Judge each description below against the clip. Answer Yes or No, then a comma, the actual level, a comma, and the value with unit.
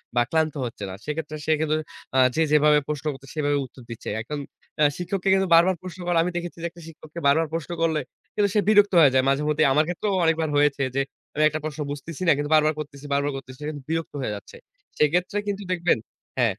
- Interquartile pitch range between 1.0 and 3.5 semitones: Yes, average, 2.7 semitones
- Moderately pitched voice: Yes, medium, 155 Hz